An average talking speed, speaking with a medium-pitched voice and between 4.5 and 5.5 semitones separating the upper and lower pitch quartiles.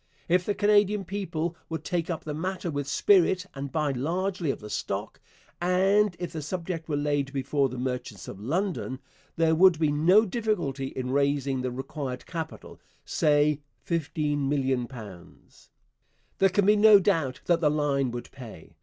Yes: average, 160 wpm; medium, 155 Hz; average, 5.1 semitones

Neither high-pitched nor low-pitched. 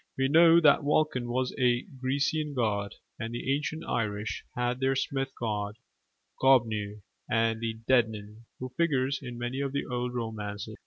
No: low, 125 Hz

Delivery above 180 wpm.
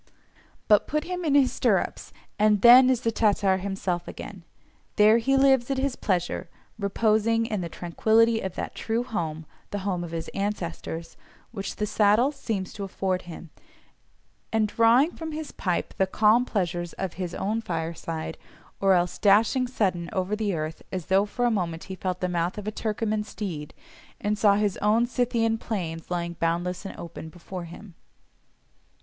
No: average, 170 wpm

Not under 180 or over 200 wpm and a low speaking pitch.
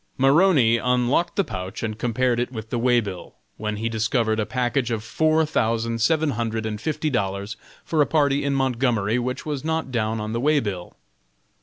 Yes: average, 190 wpm; low, 120 Hz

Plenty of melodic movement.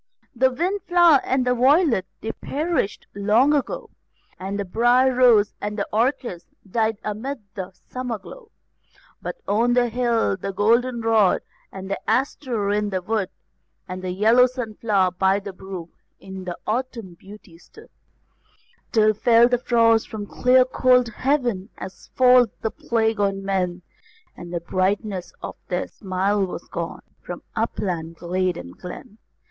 No: average, 4.5 semitones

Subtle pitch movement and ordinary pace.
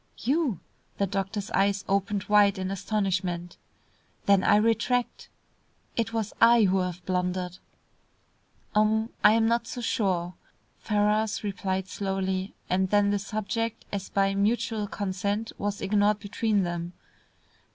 No: narrow, 2.3 semitones; slow, 130 wpm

